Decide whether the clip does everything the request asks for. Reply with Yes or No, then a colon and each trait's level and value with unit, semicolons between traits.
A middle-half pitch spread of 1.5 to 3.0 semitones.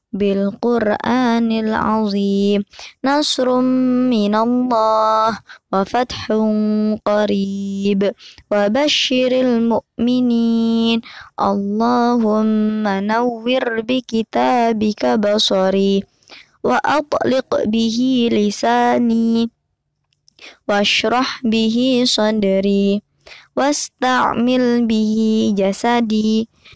Yes: average, 2.7 semitones